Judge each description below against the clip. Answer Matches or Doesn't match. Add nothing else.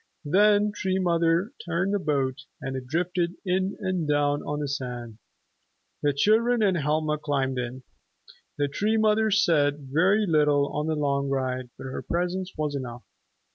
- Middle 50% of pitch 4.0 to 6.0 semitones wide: Matches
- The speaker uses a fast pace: Doesn't match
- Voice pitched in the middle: Matches